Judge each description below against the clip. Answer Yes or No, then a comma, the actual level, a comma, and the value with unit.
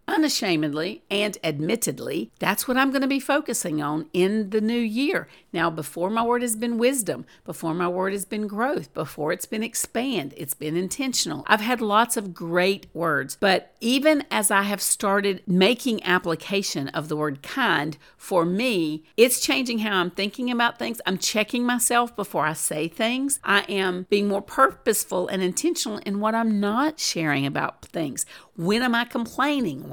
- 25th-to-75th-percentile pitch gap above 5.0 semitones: Yes, wide, 5.4 semitones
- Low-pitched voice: No, high, 210 Hz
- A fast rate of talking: No, average, 175 wpm